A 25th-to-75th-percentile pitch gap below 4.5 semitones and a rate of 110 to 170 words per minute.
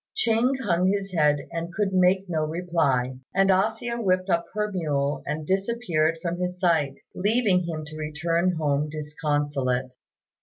Yes: average, 4.1 semitones; average, 155 wpm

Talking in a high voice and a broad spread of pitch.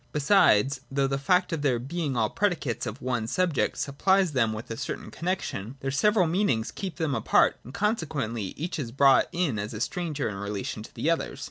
No: medium, 140 Hz; wide, 6.9 semitones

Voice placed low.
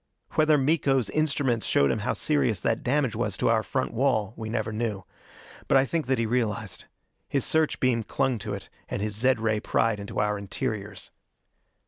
Yes: low, 115 Hz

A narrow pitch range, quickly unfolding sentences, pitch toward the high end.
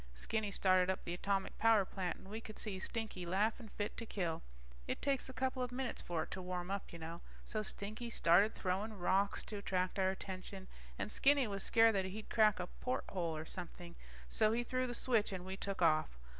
No: average, 3.4 semitones; fast, 210 wpm; high, 195 Hz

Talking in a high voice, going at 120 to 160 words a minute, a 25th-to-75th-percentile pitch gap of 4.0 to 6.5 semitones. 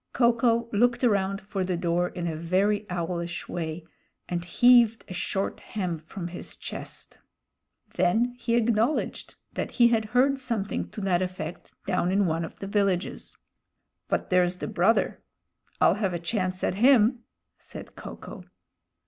Yes: high, 195 Hz; average, 155 wpm; average, 4.6 semitones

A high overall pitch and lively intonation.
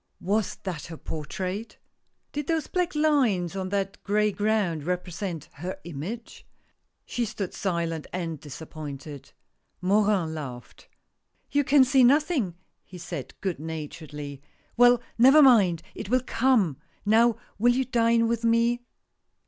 Yes: high, 200 Hz; wide, 6.3 semitones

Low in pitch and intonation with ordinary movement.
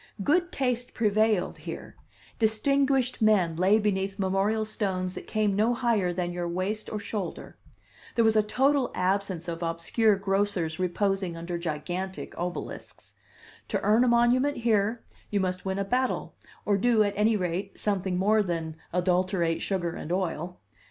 No: high, 200 Hz; average, 3.4 semitones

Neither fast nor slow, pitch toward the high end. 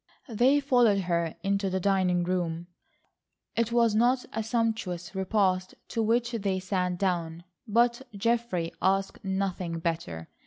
No: slow, 130 wpm; high, 195 Hz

